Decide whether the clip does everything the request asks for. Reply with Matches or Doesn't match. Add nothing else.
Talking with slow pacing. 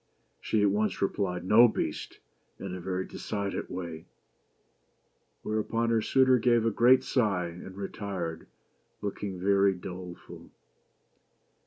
Matches